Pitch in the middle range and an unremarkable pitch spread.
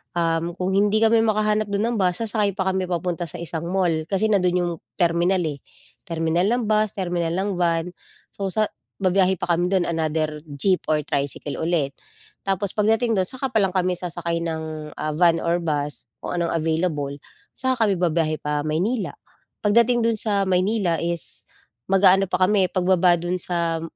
Yes: medium, 180 Hz; average, 3.2 semitones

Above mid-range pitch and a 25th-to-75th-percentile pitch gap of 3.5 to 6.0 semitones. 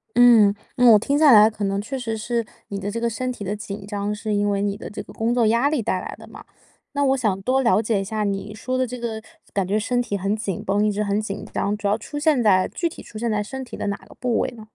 No: high, 215 Hz; average, 3.0 semitones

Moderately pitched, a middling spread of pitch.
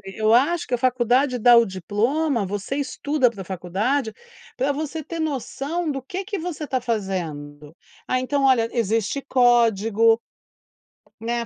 No: high, 245 Hz; average, 4.6 semitones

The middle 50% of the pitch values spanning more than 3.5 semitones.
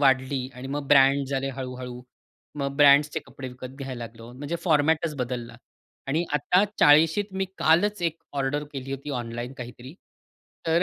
No: average, 3.0 semitones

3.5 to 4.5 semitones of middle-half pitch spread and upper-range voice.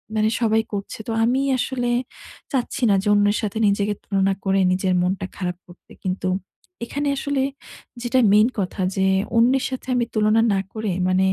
Yes: average, 3.9 semitones; high, 210 Hz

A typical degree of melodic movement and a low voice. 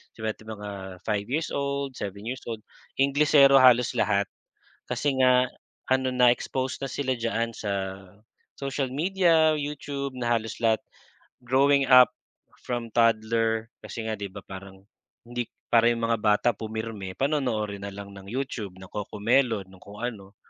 Yes: average, 4.3 semitones; low, 115 Hz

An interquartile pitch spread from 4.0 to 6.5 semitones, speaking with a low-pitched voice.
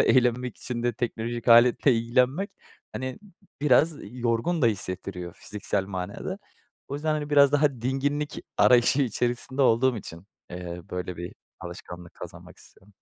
Yes: average, 5.2 semitones; low, 120 Hz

